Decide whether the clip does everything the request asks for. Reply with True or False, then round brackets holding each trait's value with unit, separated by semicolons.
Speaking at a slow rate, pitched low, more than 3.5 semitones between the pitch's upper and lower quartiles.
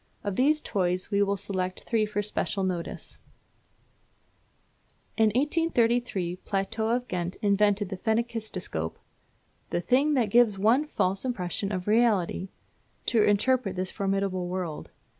False (130 wpm; 205 Hz; 3.9 semitones)